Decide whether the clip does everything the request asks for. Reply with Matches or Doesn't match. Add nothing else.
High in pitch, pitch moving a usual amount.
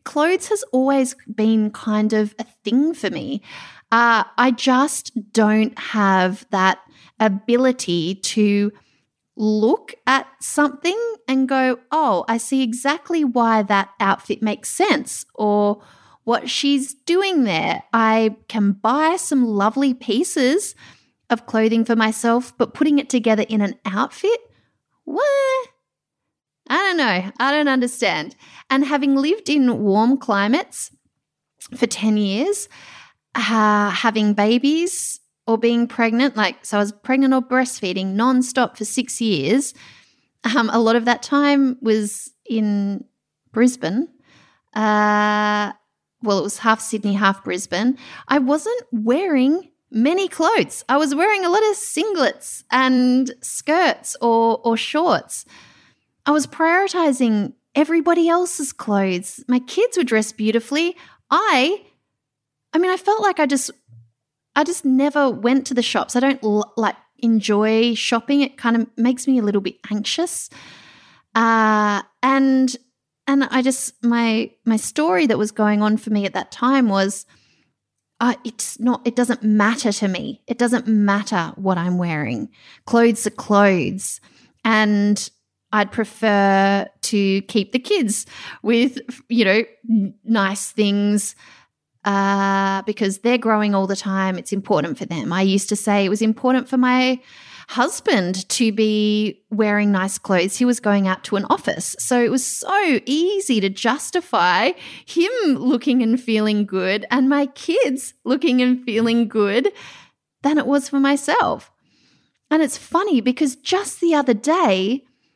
Matches